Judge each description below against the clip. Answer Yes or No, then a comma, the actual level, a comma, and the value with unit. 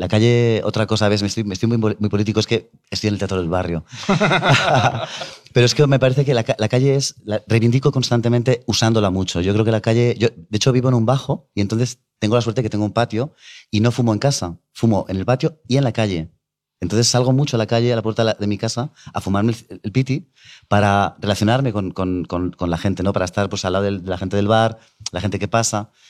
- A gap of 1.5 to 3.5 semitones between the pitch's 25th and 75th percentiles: Yes, average, 3.1 semitones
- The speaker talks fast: Yes, fast, 260 wpm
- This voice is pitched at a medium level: No, low, 110 Hz